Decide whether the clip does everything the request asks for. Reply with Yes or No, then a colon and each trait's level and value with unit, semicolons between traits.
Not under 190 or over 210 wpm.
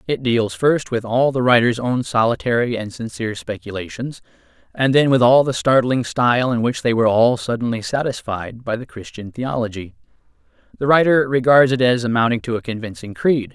No: average, 175 wpm